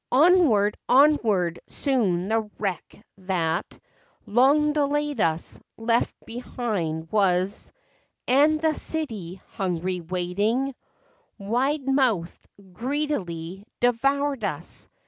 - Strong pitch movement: Yes, wide, 7.2 semitones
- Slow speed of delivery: Yes, slow, 90 wpm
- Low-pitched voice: No, high, 225 Hz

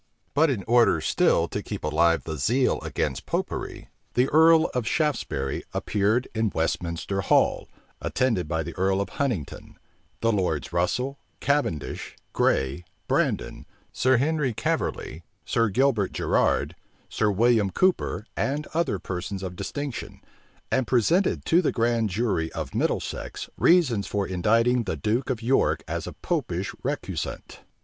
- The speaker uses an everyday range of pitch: No, wide, 6.0 semitones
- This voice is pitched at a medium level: No, low, 115 Hz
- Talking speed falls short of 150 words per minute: Yes, average, 140 wpm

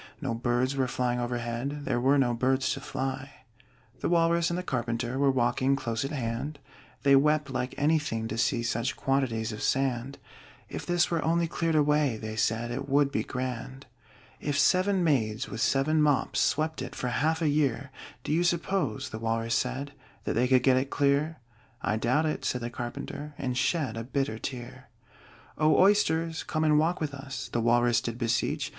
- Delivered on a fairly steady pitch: No, average, 3.9 semitones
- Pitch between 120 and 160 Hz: Yes, low, 135 Hz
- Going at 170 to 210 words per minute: Yes, average, 185 wpm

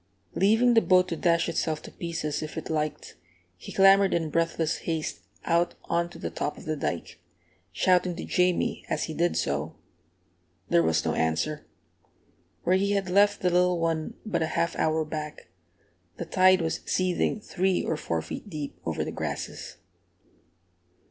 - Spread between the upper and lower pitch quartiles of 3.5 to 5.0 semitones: No, average, 2.9 semitones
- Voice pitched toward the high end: No, medium, 170 Hz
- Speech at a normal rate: Yes, average, 170 wpm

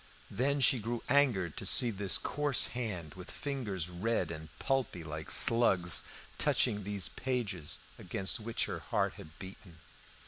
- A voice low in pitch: Yes, low, 100 Hz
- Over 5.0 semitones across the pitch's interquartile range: Yes, wide, 5.5 semitones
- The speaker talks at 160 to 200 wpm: No, average, 145 wpm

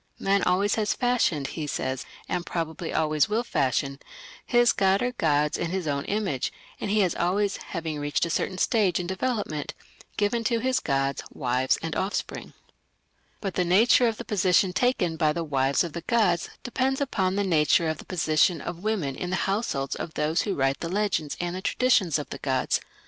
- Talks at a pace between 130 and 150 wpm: No, average, 190 wpm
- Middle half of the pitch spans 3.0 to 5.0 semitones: No, wide, 5.4 semitones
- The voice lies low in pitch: No, medium, 180 Hz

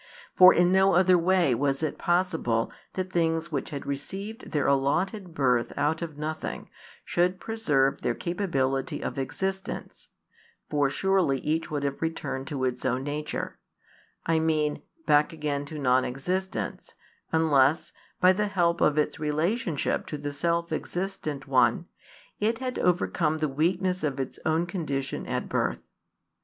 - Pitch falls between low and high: Yes, medium, 155 Hz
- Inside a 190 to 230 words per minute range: No, average, 150 wpm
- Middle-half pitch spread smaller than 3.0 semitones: No, average, 4.2 semitones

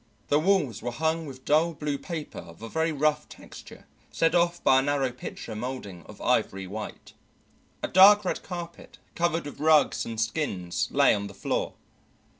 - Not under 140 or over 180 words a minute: Yes, average, 175 wpm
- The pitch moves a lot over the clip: Yes, wide, 6.4 semitones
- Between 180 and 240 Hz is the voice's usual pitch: No, medium, 145 Hz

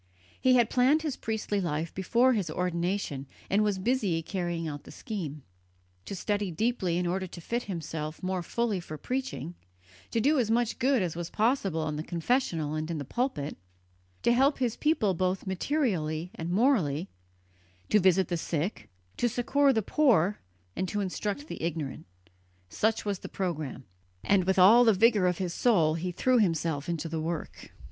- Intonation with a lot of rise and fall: Yes, wide, 6.0 semitones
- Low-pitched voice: No, high, 190 Hz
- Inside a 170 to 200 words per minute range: Yes, average, 175 wpm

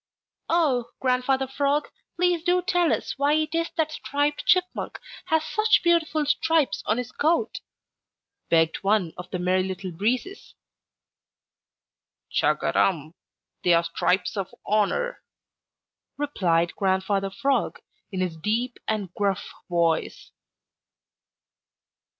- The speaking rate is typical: No, slow, 115 wpm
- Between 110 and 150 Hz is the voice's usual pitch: No, very high, 250 Hz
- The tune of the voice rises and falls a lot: Yes, wide, 9.0 semitones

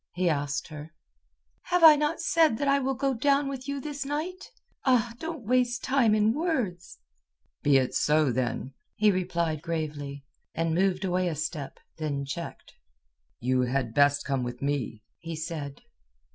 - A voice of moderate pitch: Yes, medium, 175 Hz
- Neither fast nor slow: Yes, average, 160 wpm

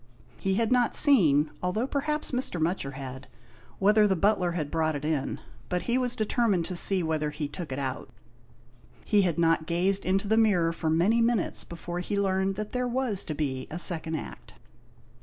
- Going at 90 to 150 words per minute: No, average, 190 wpm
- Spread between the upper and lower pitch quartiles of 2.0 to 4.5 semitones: No, average, 5.1 semitones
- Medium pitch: Yes, medium, 180 Hz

